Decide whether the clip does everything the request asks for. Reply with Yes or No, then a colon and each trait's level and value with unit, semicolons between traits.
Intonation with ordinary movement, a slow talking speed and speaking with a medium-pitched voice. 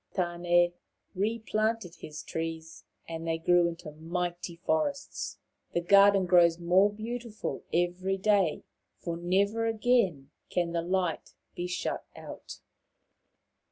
Yes: average, 3.1 semitones; slow, 120 wpm; medium, 175 Hz